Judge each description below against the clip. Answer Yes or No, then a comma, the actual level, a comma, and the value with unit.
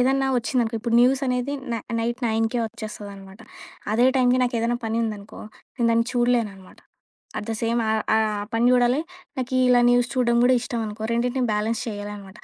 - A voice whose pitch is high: Yes, high, 235 Hz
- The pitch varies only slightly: Yes, narrow, 2.2 semitones